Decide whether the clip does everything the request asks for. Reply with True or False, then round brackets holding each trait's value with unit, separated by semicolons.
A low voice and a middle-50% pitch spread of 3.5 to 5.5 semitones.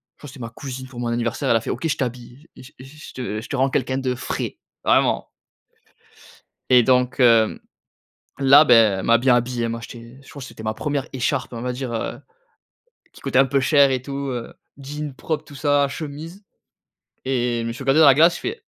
False (130 Hz; 2.9 semitones)